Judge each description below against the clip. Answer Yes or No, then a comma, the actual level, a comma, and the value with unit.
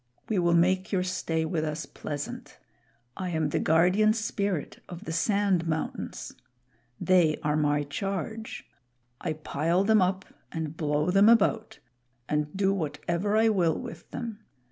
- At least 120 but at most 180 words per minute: Yes, average, 145 wpm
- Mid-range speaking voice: Yes, medium, 175 Hz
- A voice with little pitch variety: No, average, 4.0 semitones